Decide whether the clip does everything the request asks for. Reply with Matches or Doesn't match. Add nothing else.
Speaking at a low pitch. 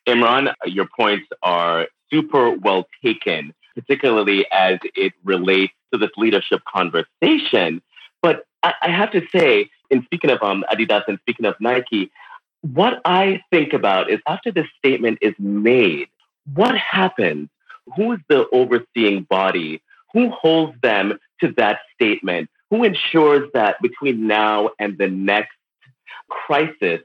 Matches